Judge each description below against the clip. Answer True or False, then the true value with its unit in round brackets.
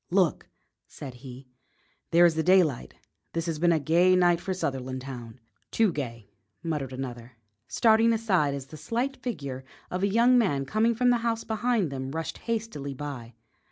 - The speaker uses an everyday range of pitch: False (8.2 semitones)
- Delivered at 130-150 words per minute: False (165 wpm)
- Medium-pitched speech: True (165 Hz)